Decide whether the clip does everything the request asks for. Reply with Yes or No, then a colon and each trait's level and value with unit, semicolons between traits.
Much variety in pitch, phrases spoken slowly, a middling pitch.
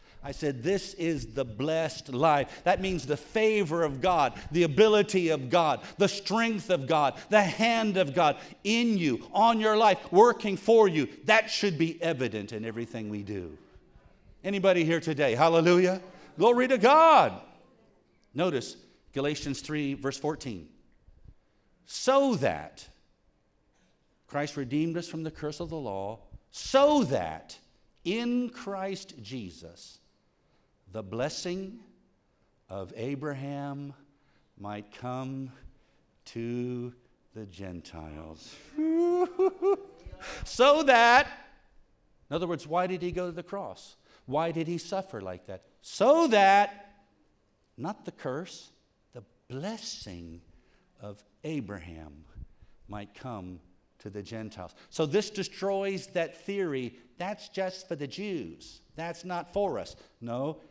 Yes: wide, 8.9 semitones; slow, 125 wpm; medium, 160 Hz